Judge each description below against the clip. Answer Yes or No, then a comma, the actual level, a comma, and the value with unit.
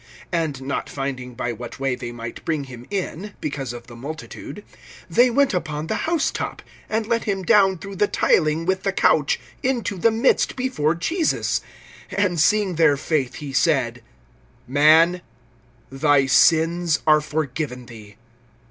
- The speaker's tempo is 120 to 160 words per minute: Yes, average, 150 wpm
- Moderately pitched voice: Yes, medium, 155 Hz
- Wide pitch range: Yes, wide, 6.2 semitones